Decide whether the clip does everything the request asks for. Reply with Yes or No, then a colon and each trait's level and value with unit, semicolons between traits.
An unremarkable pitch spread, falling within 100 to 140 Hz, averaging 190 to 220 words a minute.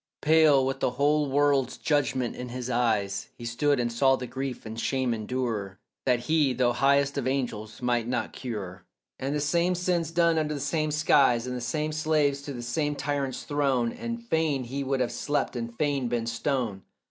Yes: average, 3.4 semitones; low, 135 Hz; average, 195 wpm